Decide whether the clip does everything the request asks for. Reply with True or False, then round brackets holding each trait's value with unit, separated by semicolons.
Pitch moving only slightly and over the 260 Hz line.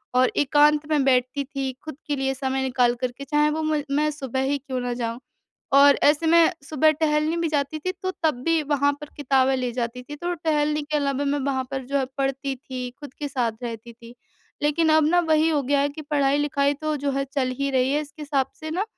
True (2.3 semitones; 285 Hz)